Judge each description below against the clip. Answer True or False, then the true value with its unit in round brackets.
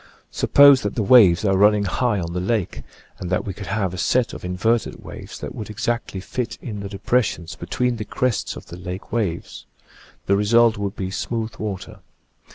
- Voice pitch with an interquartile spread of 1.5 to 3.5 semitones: False (3.9 semitones)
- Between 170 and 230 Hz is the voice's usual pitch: False (105 Hz)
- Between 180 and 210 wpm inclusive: True (190 wpm)